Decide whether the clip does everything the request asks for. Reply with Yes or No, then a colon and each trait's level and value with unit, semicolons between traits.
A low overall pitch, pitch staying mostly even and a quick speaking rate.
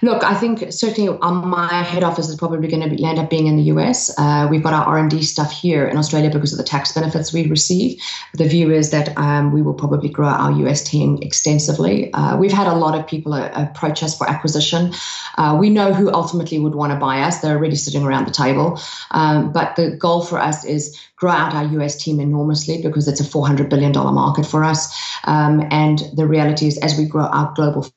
No: medium, 155 Hz; narrow, 1.8 semitones; fast, 225 wpm